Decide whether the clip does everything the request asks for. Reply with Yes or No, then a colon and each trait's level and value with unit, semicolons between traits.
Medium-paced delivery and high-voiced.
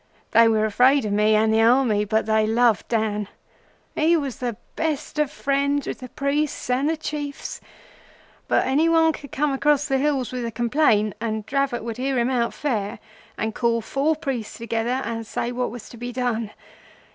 Yes: average, 190 wpm; high, 245 Hz